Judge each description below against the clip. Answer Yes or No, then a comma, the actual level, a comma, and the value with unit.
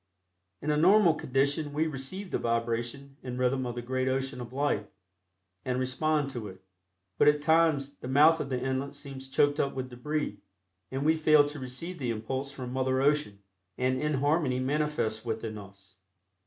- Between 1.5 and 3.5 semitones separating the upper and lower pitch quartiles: Yes, average, 2.9 semitones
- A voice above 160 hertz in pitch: No, low, 135 Hz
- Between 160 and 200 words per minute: Yes, average, 175 wpm